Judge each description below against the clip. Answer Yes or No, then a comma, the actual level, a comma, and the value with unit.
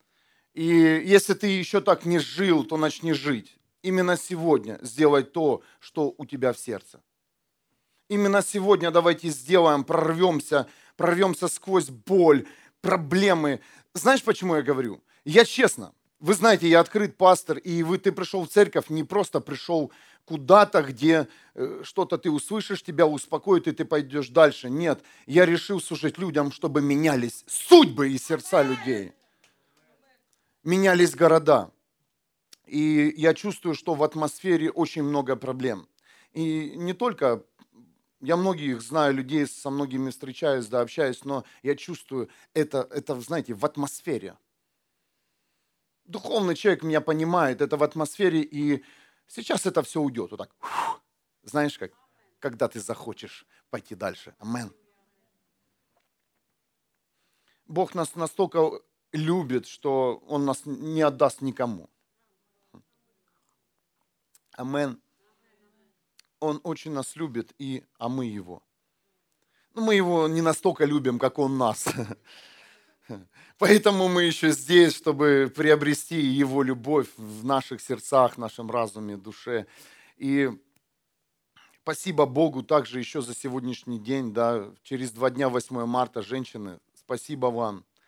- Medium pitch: Yes, medium, 155 Hz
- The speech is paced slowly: No, average, 125 wpm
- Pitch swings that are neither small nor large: Yes, average, 4.5 semitones